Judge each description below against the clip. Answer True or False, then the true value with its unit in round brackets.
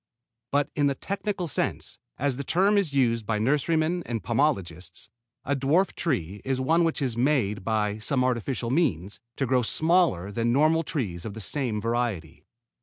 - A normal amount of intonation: False (5.9 semitones)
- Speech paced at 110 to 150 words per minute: False (170 wpm)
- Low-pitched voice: True (130 Hz)